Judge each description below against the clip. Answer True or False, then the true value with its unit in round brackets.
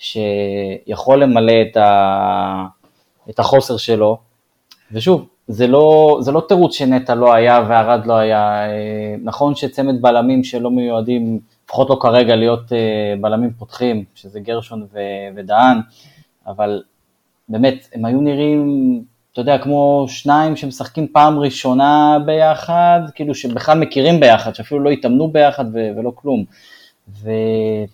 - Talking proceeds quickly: False (125 wpm)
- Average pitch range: True (4.3 semitones)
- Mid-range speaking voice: False (120 Hz)